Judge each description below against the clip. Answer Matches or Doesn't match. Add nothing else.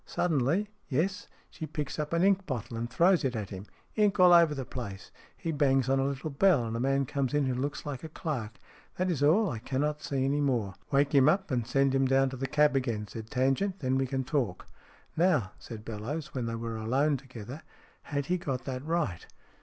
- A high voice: Doesn't match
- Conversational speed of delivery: Doesn't match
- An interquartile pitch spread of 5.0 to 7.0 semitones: Doesn't match